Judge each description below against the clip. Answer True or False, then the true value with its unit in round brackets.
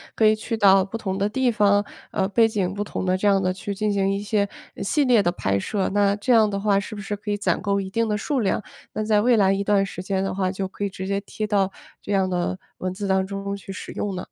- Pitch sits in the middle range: False (200 Hz)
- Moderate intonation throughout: False (1.5 semitones)